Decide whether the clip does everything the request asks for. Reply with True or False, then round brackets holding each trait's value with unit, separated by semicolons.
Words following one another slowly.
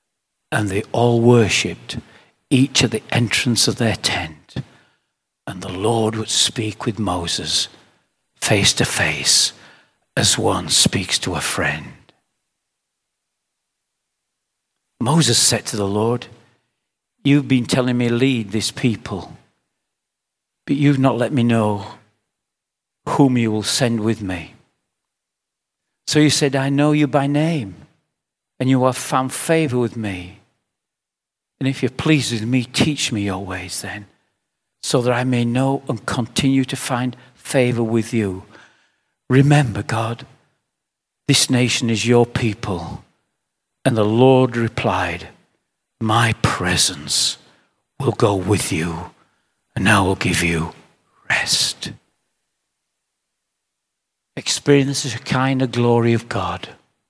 True (125 wpm)